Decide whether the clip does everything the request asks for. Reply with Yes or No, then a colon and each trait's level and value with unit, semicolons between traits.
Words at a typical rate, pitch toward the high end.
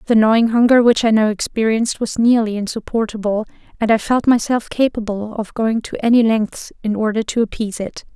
Yes: average, 185 wpm; high, 220 Hz